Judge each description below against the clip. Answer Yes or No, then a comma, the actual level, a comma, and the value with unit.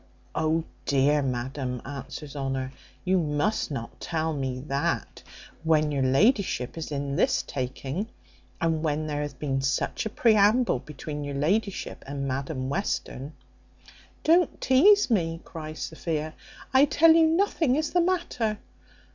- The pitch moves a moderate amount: No, wide, 7.5 semitones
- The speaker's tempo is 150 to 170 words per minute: No, average, 140 wpm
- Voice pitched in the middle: Yes, medium, 155 Hz